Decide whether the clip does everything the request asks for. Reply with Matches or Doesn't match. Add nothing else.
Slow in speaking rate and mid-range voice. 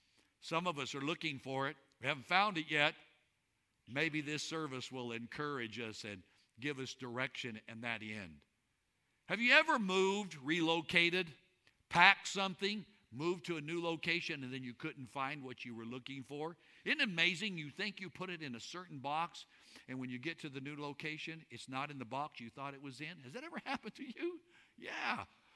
Doesn't match